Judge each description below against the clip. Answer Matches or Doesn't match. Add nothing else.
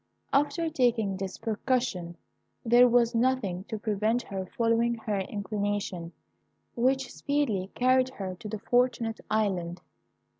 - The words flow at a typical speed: Doesn't match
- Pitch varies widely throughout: Doesn't match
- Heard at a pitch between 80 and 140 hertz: Doesn't match